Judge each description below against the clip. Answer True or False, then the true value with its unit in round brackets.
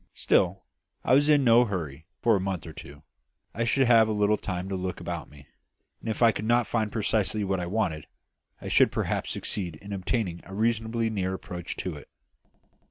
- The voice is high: False (100 Hz)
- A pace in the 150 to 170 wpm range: False (200 wpm)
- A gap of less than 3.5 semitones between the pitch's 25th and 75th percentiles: False (4.2 semitones)